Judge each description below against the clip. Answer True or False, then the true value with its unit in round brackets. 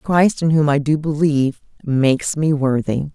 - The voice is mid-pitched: True (150 Hz)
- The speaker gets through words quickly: False (170 wpm)